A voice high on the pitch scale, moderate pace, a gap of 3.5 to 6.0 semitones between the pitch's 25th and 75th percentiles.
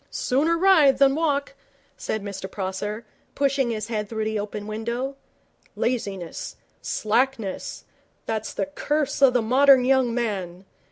No: high, 235 Hz; slow, 130 wpm; average, 4.6 semitones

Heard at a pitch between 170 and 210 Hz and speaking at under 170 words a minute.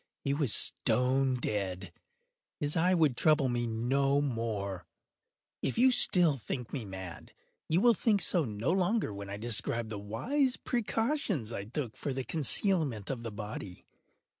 No: low, 130 Hz; average, 155 wpm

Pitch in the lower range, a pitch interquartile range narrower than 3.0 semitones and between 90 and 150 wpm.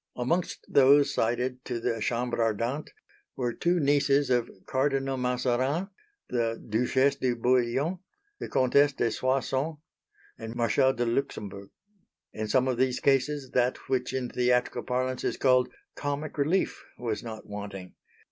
Yes: low, 125 Hz; narrow, 2.4 semitones; average, 140 wpm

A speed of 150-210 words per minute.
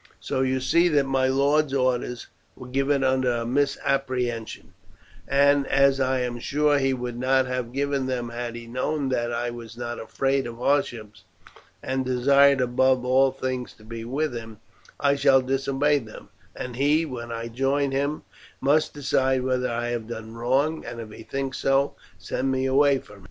Yes: average, 180 wpm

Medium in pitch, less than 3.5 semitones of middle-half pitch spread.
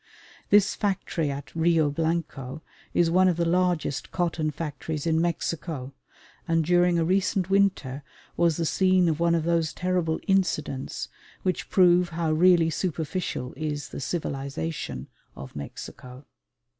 Yes: medium, 165 Hz; average, 2.9 semitones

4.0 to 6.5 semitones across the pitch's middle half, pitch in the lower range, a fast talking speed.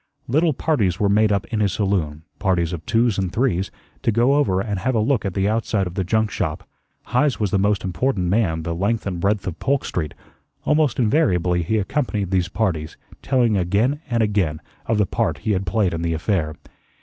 Yes: average, 4.3 semitones; low, 100 Hz; fast, 210 wpm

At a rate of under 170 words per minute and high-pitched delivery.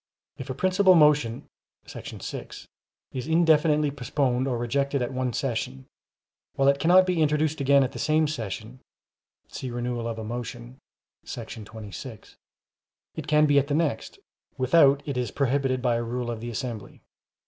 No: average, 160 wpm; low, 130 Hz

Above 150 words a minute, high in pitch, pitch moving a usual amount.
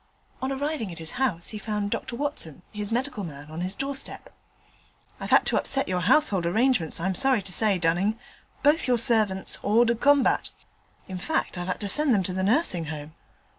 No: average, 195 wpm; high, 210 Hz; wide, 6.5 semitones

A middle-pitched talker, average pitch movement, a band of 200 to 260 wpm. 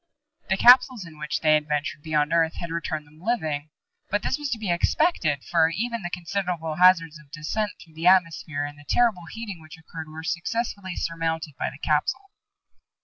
No: medium, 165 Hz; average, 3.9 semitones; average, 190 wpm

